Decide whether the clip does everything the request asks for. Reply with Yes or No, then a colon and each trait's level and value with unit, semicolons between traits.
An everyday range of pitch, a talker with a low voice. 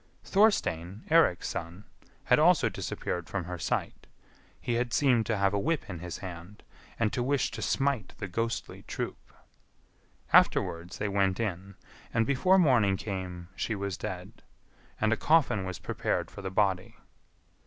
Yes: average, 4.4 semitones; low, 100 Hz